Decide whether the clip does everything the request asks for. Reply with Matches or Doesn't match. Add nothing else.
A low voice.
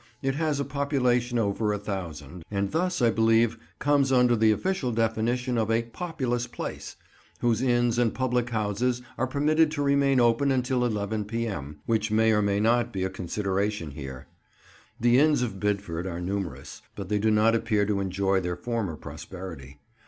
Matches